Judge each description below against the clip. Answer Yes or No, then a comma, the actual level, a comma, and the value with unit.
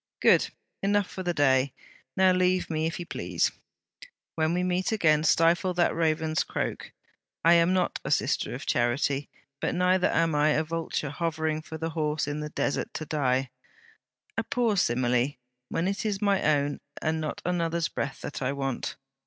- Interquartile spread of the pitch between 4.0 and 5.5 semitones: No, average, 3.4 semitones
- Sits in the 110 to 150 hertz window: No, medium, 160 Hz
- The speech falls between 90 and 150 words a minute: No, average, 175 wpm